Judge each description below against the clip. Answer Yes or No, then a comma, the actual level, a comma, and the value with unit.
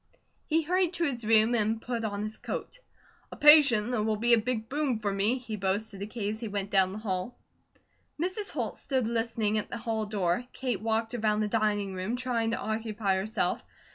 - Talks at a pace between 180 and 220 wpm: Yes, fast, 205 wpm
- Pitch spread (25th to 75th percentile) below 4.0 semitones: Yes, narrow, 2.6 semitones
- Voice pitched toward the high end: Yes, high, 220 Hz